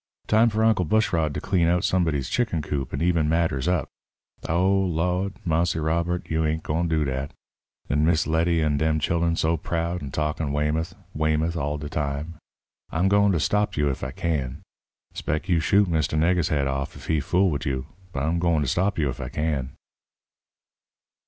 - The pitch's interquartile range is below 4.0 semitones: Yes, average, 2.8 semitones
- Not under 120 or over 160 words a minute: No, average, 185 wpm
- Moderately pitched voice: No, very low, 80 Hz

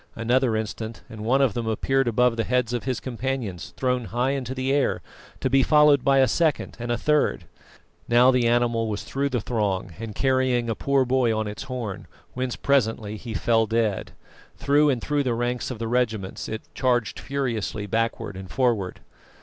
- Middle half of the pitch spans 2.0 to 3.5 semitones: Yes, average, 2.9 semitones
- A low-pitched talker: Yes, low, 120 Hz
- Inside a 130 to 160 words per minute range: No, average, 190 wpm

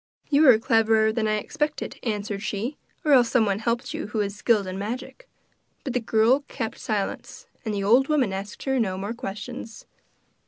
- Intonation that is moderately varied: Yes, average, 3.3 semitones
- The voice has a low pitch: No, high, 220 Hz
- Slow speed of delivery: No, average, 185 wpm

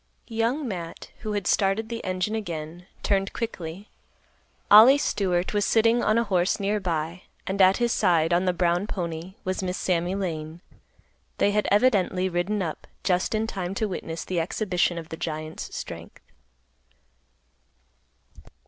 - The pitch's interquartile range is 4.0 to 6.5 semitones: No, average, 3.4 semitones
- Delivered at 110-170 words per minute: Yes, average, 150 wpm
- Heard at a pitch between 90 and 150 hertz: No, medium, 185 Hz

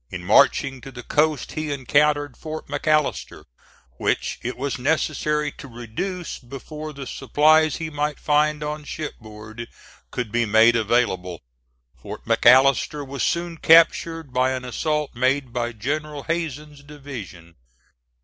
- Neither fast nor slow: No, slow, 130 wpm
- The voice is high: No, medium, 140 Hz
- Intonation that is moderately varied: Yes, average, 3.9 semitones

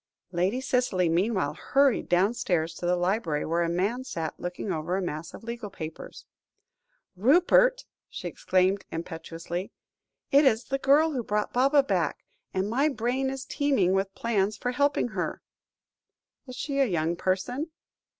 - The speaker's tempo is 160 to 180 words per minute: No, average, 150 wpm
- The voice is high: Yes, high, 205 Hz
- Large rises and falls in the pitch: Yes, wide, 6.9 semitones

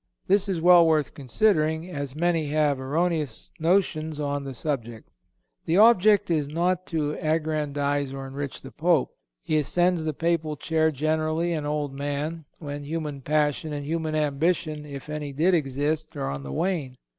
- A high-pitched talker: No, medium, 155 Hz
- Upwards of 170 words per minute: No, average, 160 wpm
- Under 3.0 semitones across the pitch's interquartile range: Yes, narrow, 2.6 semitones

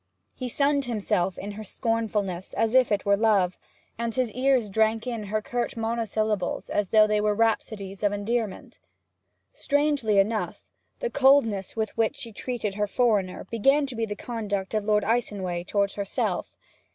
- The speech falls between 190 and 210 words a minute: No, average, 165 wpm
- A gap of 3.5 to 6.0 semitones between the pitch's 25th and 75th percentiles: No, average, 2.7 semitones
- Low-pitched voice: No, high, 220 Hz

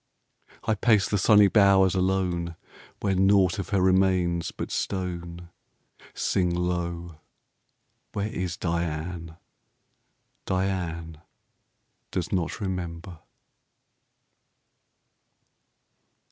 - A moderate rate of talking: No, slow, 80 wpm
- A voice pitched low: Yes, very low, 90 Hz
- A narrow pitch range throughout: Yes, narrow, 2.1 semitones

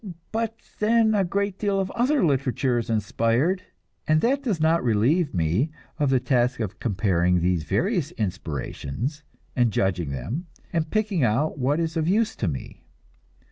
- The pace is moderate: Yes, average, 160 wpm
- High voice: No, medium, 140 Hz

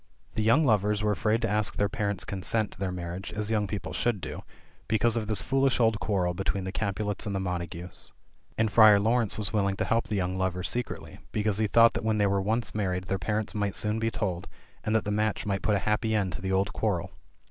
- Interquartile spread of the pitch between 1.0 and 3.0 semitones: Yes, narrow, 2.4 semitones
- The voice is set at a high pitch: No, low, 105 Hz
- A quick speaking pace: Yes, fast, 235 wpm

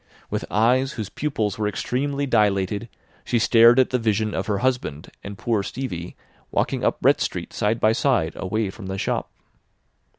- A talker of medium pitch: No, low, 110 Hz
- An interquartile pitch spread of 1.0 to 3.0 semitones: No, average, 3.9 semitones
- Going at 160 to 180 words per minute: Yes, average, 170 wpm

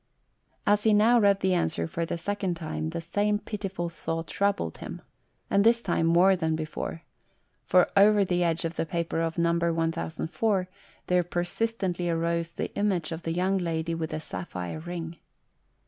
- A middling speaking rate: Yes, average, 170 wpm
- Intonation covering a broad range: No, average, 3.1 semitones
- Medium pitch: Yes, medium, 170 Hz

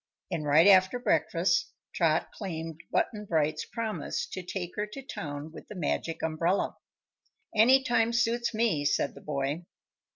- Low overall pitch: No, medium, 175 Hz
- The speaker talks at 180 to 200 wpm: No, average, 150 wpm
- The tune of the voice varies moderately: No, wide, 5.7 semitones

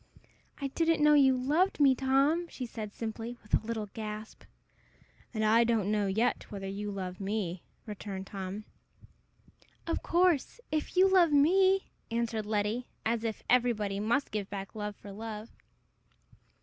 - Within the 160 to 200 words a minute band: No, average, 150 wpm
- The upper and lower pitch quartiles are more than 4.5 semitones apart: Yes, average, 4.9 semitones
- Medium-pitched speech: No, high, 225 Hz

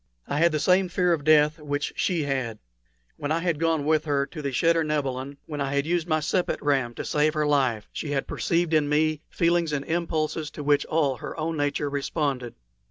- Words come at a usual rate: No, fast, 210 wpm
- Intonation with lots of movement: No, narrow, 2.4 semitones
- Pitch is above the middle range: No, medium, 150 Hz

